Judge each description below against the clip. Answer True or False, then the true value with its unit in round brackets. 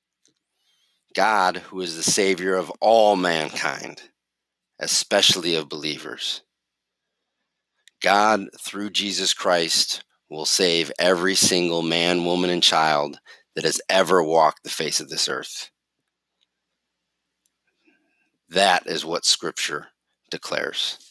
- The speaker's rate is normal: False (105 wpm)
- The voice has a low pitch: True (90 Hz)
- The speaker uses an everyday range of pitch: True (3.6 semitones)